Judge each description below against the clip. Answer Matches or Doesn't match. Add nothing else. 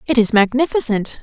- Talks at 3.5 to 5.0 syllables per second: Doesn't match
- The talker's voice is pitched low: Doesn't match